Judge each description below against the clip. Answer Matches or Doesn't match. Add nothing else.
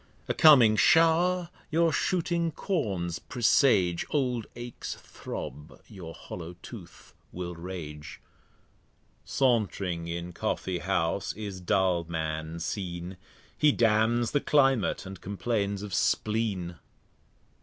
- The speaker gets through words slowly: Matches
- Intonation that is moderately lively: Doesn't match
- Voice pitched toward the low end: Matches